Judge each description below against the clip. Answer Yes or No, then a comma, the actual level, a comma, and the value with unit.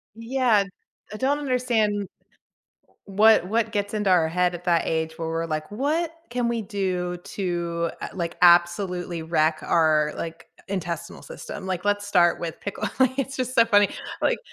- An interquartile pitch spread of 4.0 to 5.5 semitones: Yes, average, 4.8 semitones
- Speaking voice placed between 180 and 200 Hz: Yes, high, 190 Hz